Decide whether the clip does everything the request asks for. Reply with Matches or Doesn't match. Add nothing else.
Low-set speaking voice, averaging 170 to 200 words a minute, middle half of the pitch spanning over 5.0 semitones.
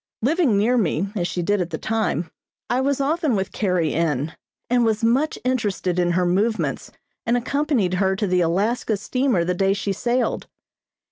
Doesn't match